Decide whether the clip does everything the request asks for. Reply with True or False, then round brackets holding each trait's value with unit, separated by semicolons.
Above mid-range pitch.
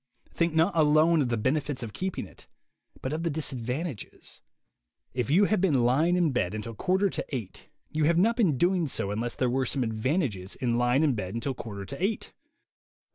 False (140 Hz)